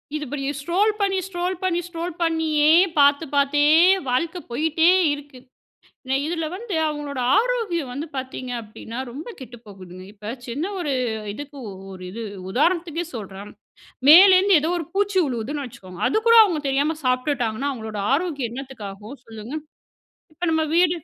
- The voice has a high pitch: Yes, very high, 295 Hz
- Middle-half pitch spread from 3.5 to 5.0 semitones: No, wide, 5.5 semitones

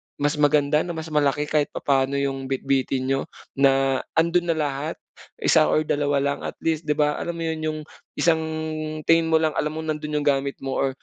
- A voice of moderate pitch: Yes, medium, 150 Hz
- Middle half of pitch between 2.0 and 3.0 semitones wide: Yes, narrow, 2.4 semitones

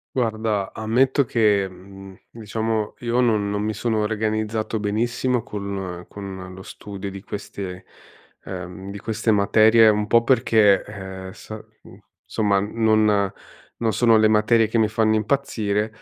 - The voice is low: Yes, low, 105 Hz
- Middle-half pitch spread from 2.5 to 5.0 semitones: No, narrow, 2.0 semitones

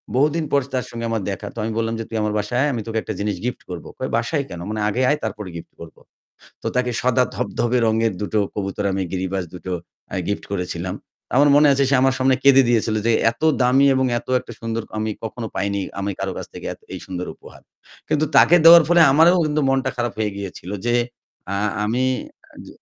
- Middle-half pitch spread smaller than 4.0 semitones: No, average, 4.3 semitones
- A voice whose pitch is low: Yes, low, 115 Hz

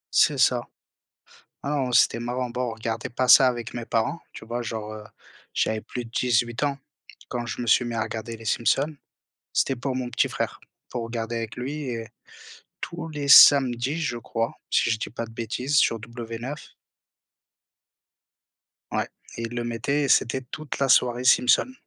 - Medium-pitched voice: No, low, 120 Hz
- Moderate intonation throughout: No, narrow, 2.3 semitones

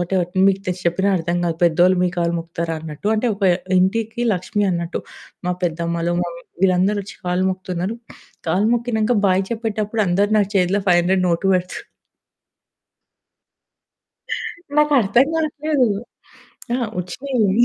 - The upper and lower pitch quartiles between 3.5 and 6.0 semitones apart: Yes, average, 3.8 semitones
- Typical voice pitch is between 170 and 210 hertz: Yes, medium, 185 Hz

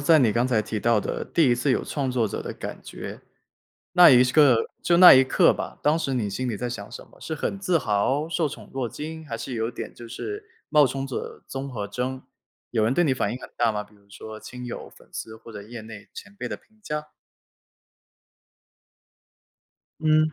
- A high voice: No, low, 125 Hz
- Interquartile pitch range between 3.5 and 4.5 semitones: No, average, 5.0 semitones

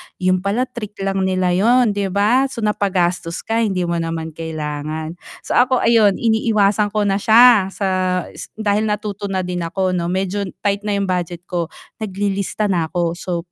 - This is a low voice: No, high, 195 Hz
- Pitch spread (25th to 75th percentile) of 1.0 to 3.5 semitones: Yes, average, 3.1 semitones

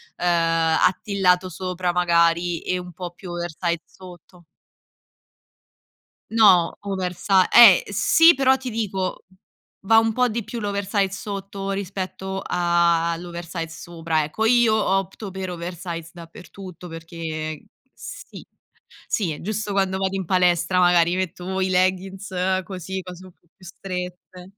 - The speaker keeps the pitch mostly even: Yes, narrow, 2.2 semitones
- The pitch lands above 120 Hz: Yes, medium, 185 Hz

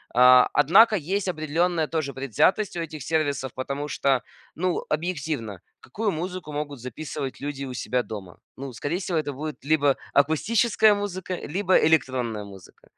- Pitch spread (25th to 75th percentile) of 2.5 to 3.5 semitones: No, average, 4.8 semitones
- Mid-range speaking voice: Yes, medium, 150 Hz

